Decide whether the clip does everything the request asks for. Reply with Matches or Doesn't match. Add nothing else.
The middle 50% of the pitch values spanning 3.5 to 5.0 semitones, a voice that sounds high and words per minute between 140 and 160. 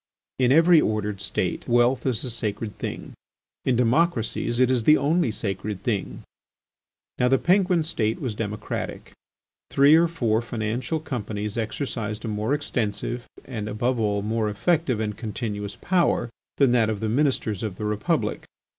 Doesn't match